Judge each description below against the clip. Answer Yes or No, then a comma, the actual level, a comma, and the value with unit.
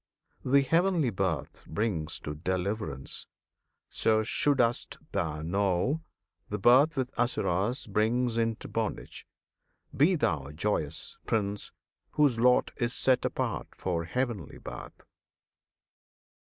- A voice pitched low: Yes, low, 110 Hz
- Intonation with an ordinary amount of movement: No, wide, 6.0 semitones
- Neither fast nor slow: No, slow, 110 wpm